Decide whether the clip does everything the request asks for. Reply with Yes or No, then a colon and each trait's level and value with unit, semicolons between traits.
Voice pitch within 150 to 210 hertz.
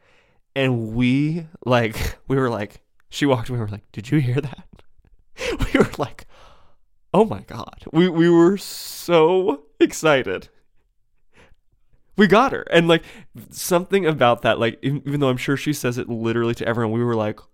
No: low, 135 Hz